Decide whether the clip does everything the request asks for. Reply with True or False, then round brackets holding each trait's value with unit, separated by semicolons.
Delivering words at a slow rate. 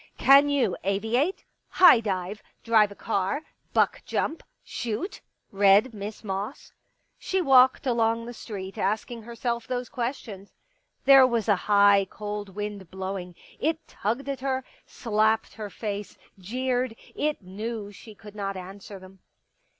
False (155 wpm)